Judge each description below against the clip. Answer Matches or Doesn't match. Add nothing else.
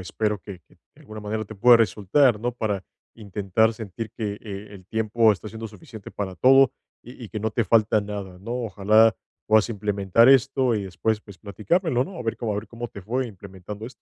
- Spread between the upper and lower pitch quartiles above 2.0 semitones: Matches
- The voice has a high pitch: Doesn't match